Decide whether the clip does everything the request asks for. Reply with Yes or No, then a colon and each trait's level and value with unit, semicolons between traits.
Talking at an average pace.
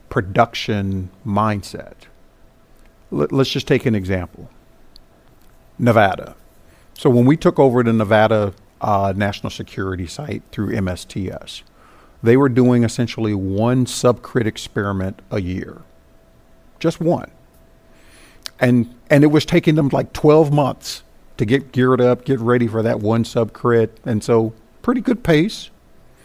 No: slow, 130 wpm